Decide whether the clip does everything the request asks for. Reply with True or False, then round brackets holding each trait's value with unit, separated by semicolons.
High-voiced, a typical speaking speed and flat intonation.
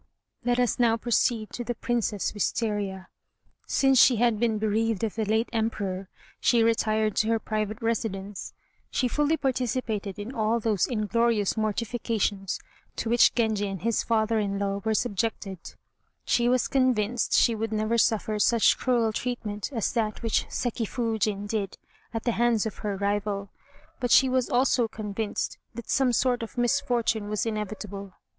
True (220 Hz; 160 wpm; 2.3 semitones)